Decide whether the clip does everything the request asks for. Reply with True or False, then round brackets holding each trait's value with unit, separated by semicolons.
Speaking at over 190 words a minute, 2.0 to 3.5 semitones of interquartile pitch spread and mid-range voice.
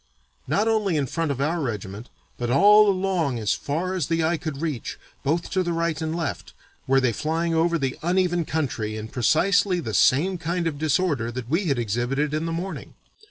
False (200 wpm; 4.7 semitones; 160 Hz)